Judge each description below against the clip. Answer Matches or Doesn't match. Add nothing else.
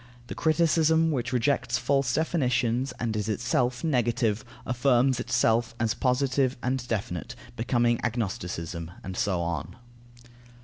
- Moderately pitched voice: Doesn't match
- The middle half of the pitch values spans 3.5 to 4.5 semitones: Doesn't match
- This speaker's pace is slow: Matches